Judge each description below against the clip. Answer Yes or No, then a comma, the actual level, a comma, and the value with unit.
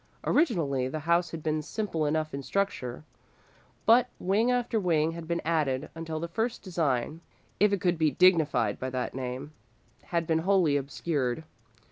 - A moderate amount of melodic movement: Yes, average, 4.2 semitones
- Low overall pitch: No, medium, 160 Hz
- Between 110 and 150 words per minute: No, average, 160 wpm